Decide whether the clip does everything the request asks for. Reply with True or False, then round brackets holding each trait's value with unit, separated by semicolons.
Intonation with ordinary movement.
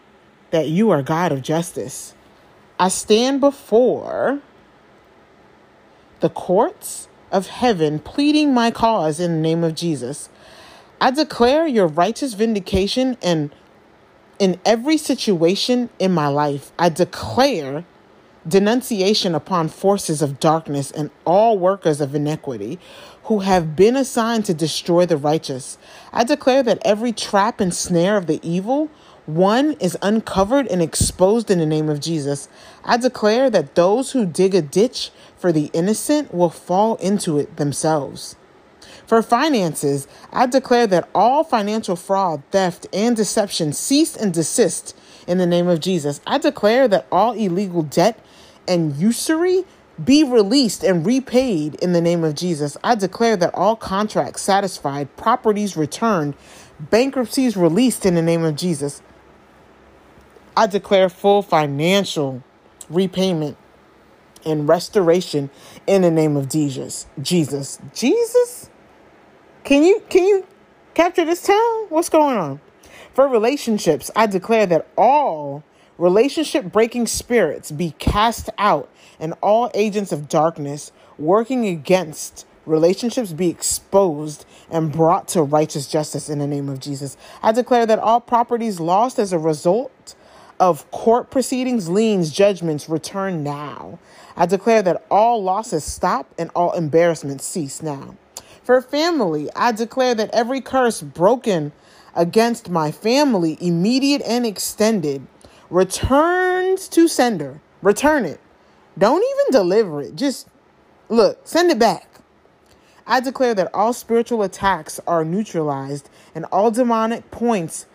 False (6.7 semitones)